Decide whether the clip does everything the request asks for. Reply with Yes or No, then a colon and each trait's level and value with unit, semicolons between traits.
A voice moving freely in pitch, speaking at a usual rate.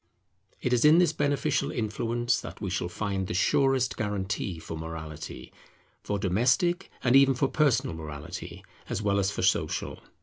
Yes: wide, 6.1 semitones; average, 160 wpm